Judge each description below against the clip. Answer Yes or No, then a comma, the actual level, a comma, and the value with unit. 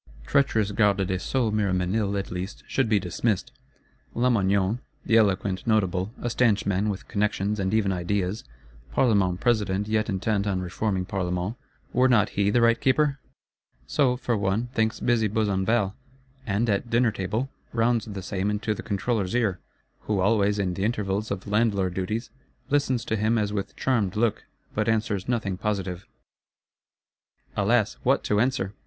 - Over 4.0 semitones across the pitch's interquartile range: No, average, 2.9 semitones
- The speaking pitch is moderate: No, low, 105 Hz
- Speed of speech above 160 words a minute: No, average, 155 wpm